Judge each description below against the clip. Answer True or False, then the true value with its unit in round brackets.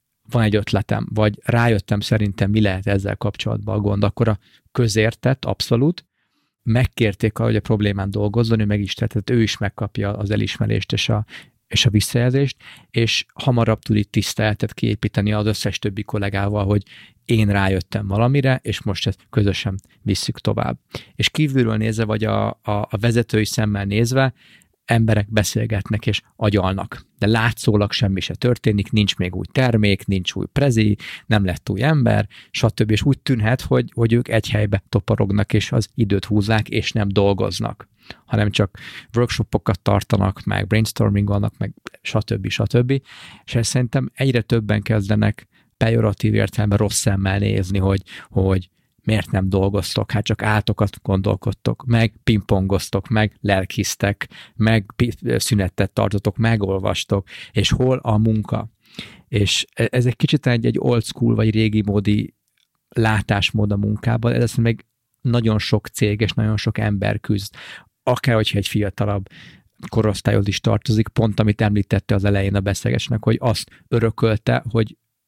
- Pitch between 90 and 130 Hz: True (110 Hz)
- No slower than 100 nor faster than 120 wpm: False (145 wpm)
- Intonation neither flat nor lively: False (2.3 semitones)